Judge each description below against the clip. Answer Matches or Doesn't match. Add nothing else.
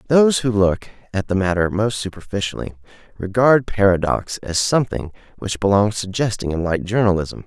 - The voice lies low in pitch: Matches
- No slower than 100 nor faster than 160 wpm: Matches